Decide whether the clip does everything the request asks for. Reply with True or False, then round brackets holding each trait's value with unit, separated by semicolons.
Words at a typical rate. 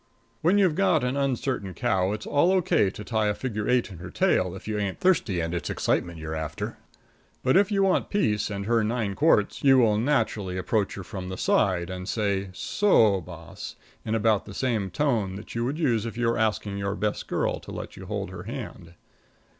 False (210 wpm)